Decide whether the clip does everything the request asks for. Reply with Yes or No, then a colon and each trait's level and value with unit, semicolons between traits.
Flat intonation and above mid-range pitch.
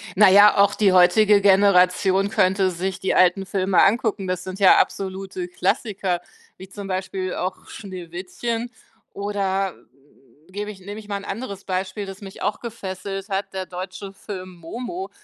Yes: narrow, 1.6 semitones; high, 195 Hz